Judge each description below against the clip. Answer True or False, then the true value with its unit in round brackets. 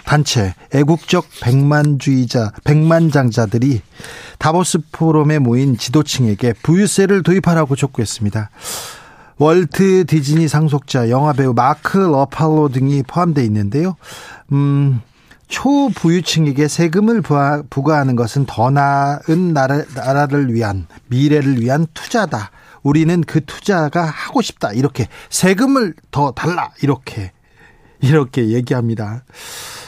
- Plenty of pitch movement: False (4.0 semitones)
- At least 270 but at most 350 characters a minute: True (275 characters per minute)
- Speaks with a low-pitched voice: False (145 Hz)